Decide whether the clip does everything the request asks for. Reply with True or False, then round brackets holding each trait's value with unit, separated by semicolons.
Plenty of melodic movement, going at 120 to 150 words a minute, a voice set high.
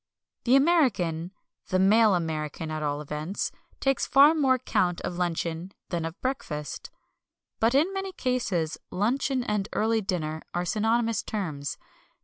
True (7.5 semitones; 135 wpm; 195 Hz)